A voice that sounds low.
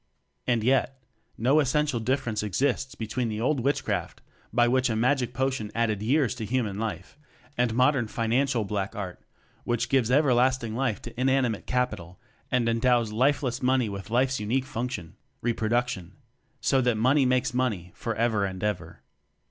Yes: low, 120 Hz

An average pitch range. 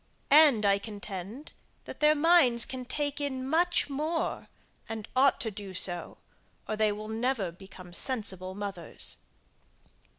No: wide, 6.1 semitones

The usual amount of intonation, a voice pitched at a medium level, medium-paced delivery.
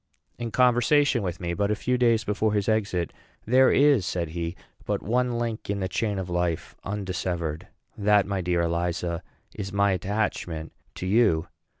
No: average, 4.4 semitones; low, 100 Hz; average, 170 wpm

